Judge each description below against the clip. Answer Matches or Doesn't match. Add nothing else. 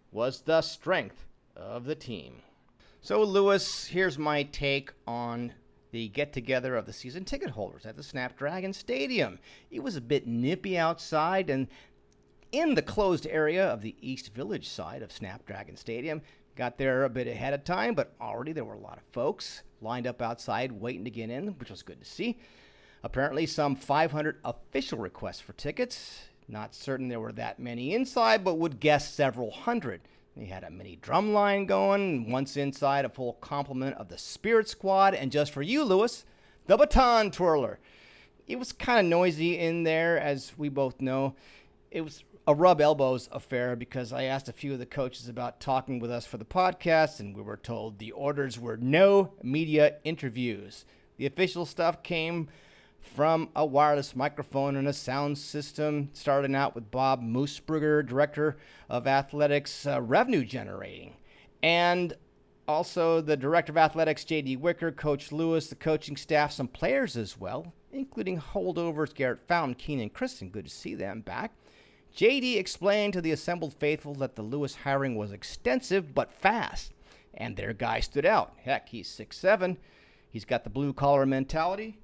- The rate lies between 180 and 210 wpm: Doesn't match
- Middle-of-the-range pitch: Matches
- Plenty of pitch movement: Doesn't match